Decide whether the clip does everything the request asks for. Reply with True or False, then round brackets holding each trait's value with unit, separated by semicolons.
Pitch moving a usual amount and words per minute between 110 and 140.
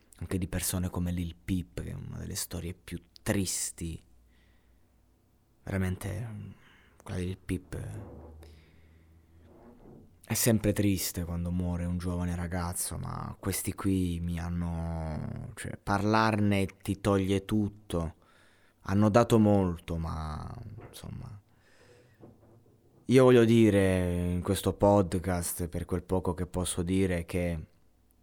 True (3.7 semitones; 115 wpm)